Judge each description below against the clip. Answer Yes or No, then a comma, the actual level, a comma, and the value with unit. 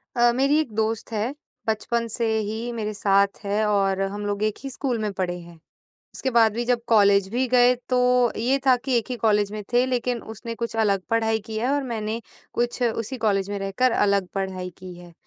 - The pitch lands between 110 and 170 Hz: No, high, 220 Hz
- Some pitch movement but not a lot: Yes, average, 3.2 semitones